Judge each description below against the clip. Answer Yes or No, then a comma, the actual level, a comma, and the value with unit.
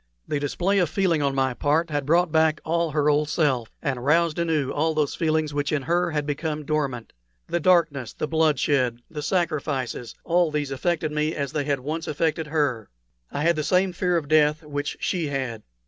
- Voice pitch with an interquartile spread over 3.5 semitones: No, narrow, 2.4 semitones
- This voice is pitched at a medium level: Yes, medium, 150 Hz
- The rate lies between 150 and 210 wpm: Yes, average, 195 wpm